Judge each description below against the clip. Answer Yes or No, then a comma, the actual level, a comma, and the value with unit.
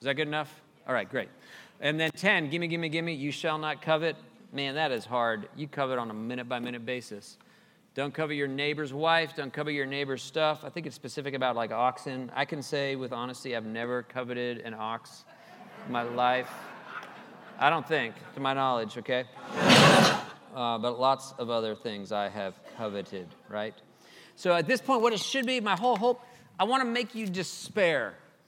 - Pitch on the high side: No, medium, 140 Hz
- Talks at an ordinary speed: Yes, average, 195 wpm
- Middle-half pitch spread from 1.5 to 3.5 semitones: No, average, 4.9 semitones